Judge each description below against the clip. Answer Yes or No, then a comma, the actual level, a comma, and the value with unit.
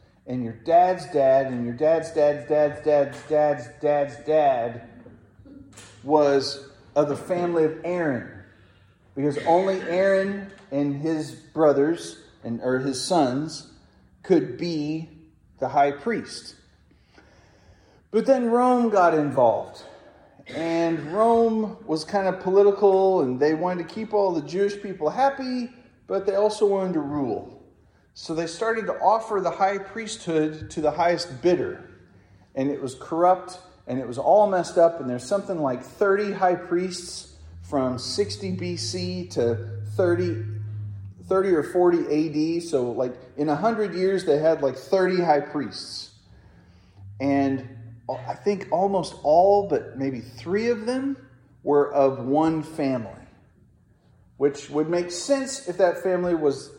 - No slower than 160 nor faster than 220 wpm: No, average, 145 wpm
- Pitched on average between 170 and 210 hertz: No, medium, 150 Hz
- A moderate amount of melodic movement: No, wide, 6.3 semitones